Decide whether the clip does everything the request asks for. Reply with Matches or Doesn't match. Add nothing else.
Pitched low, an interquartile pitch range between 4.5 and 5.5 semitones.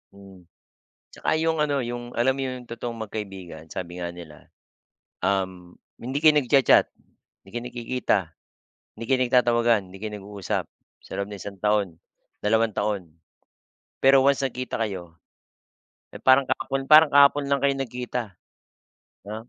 Matches